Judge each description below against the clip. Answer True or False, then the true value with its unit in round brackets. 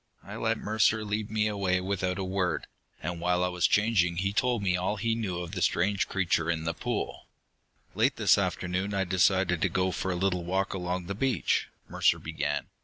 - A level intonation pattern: True (2.3 semitones)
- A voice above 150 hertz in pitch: False (95 Hz)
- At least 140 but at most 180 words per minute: False (200 wpm)